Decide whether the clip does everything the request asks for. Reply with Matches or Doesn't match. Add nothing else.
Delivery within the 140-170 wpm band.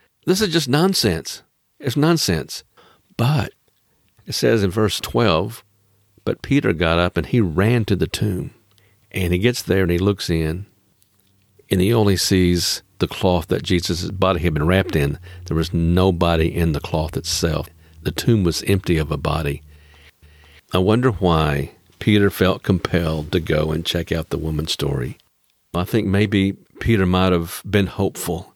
Matches